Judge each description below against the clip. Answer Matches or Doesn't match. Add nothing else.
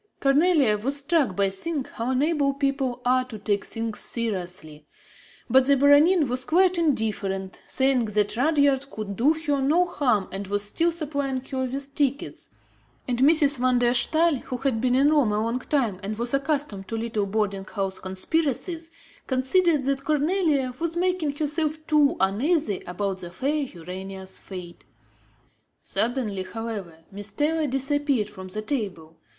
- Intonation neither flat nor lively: Doesn't match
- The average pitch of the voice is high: Matches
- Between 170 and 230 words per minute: Doesn't match